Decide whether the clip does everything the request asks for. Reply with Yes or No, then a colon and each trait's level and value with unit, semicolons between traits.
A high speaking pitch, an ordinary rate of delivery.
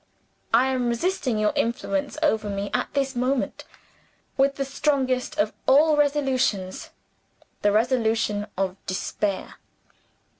No: very high, 250 Hz; slow, 115 wpm